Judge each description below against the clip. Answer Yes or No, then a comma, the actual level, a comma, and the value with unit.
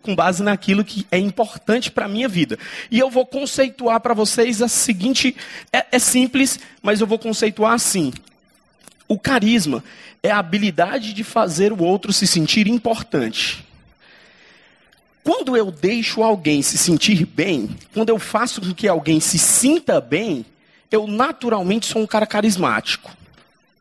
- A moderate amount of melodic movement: Yes, average, 3.6 semitones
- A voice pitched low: No, high, 220 Hz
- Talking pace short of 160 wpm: Yes, average, 150 wpm